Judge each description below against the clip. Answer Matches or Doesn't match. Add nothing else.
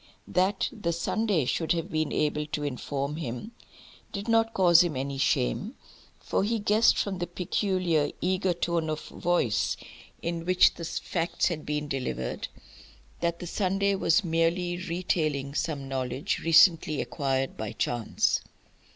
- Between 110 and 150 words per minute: Matches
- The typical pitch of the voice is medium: Matches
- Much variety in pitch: Doesn't match